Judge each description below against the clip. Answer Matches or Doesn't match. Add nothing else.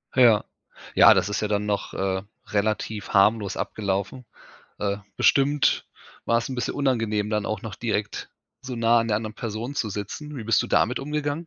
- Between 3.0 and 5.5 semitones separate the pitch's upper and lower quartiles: Matches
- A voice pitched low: Matches